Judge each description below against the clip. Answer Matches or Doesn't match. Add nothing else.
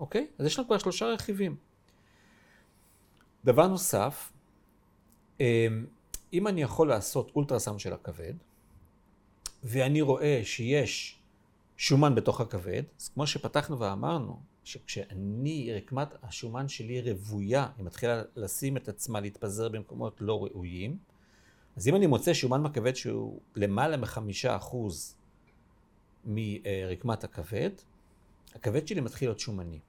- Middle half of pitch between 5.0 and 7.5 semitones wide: Matches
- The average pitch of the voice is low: Matches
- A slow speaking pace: Doesn't match